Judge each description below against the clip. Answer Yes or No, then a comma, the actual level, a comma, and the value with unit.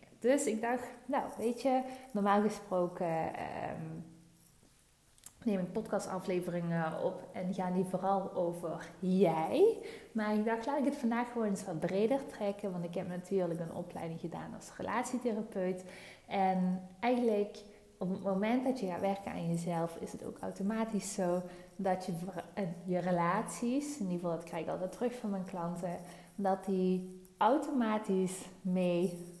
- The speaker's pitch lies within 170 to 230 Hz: Yes, high, 190 Hz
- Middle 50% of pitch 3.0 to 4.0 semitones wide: Yes, average, 3.7 semitones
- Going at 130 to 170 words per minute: Yes, average, 155 wpm